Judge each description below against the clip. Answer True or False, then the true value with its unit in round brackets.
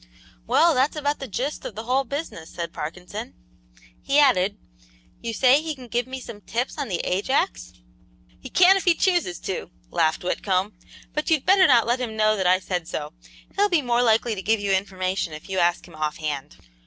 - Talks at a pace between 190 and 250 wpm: True (200 wpm)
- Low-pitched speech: False (220 Hz)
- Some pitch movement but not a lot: False (6.9 semitones)